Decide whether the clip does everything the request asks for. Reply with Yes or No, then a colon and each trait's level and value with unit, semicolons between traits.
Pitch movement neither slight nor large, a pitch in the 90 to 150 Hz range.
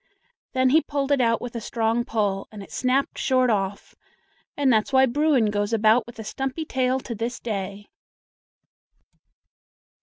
No: average, 3.5 semitones; high, 240 Hz